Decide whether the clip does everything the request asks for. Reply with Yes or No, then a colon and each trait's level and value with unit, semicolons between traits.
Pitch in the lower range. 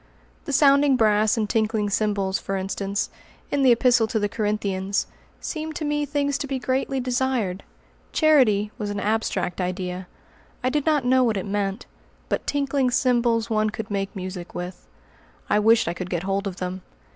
No: high, 215 Hz